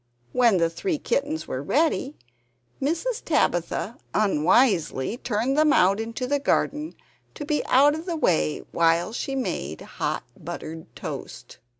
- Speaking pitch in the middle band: No, very high, 250 Hz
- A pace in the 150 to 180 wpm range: No, slow, 135 wpm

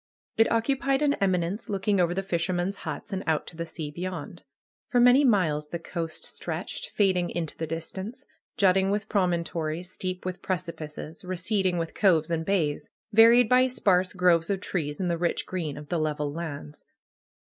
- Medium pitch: Yes, medium, 180 Hz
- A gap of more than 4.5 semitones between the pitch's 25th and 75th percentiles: No, average, 3.3 semitones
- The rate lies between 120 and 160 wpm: No, average, 175 wpm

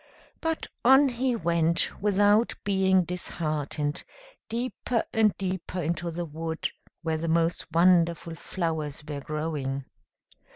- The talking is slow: Yes, slow, 115 wpm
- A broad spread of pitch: No, average, 3.9 semitones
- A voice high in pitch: No, medium, 170 Hz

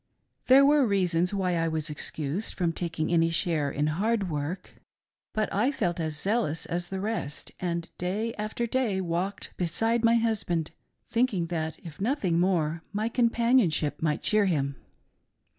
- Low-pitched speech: No, medium, 180 Hz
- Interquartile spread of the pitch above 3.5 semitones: Yes, average, 5.1 semitones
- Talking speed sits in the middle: Yes, average, 160 wpm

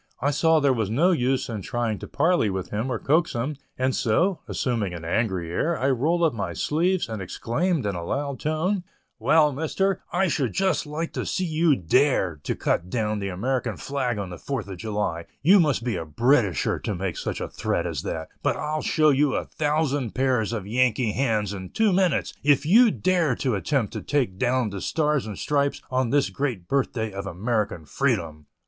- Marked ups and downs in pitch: Yes, wide, 6.6 semitones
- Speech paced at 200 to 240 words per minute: Yes, fast, 205 wpm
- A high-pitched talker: No, low, 130 Hz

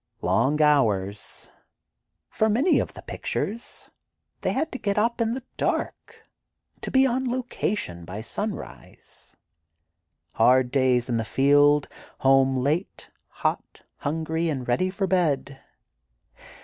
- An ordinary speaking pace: No, slow, 125 wpm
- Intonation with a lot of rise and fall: Yes, wide, 8.8 semitones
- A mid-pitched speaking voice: Yes, medium, 145 Hz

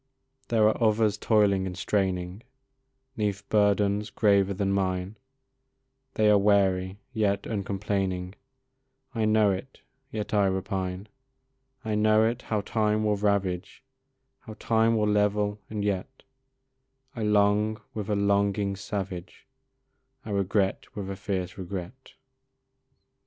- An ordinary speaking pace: No, slow, 120 wpm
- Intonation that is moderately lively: No, narrow, 1.7 semitones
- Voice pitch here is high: No, low, 100 Hz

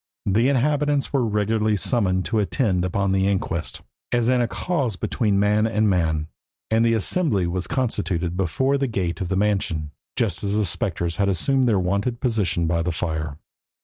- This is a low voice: Yes, low, 100 Hz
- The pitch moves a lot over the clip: No, average, 4.6 semitones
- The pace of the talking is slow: No, average, 180 wpm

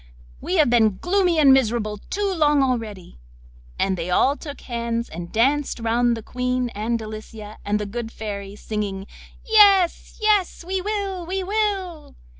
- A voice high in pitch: Yes, high, 245 Hz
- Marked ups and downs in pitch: Yes, wide, 8.9 semitones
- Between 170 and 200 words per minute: No, average, 155 wpm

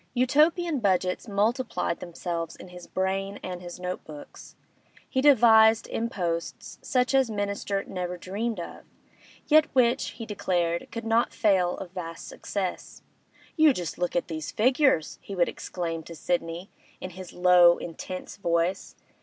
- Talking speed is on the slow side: No, average, 145 wpm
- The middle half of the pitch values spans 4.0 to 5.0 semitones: Yes, average, 4.7 semitones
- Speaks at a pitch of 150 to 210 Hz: Yes, high, 190 Hz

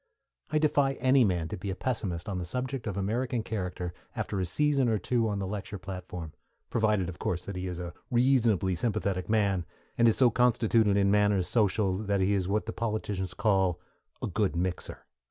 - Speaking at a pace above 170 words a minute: Yes, average, 195 wpm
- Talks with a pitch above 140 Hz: No, low, 100 Hz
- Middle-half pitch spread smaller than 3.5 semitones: No, average, 3.9 semitones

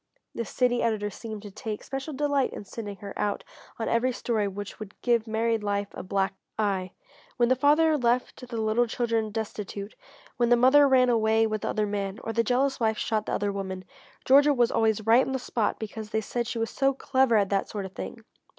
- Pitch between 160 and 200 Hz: No, high, 225 Hz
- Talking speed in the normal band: No, fast, 215 wpm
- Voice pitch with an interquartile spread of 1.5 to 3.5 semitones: Yes, average, 3.0 semitones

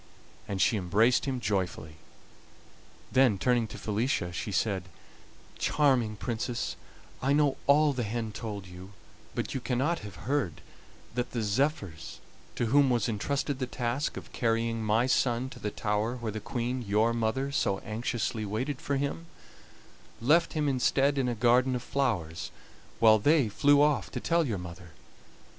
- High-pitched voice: No, low, 120 Hz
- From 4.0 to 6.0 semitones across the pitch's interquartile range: Yes, average, 4.4 semitones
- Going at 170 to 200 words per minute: No, average, 155 wpm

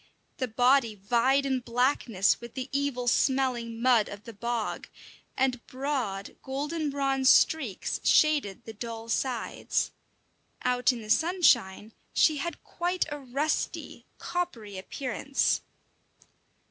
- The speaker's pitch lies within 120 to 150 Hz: No, very high, 255 Hz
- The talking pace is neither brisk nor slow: No, slow, 120 wpm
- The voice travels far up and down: No, average, 3.4 semitones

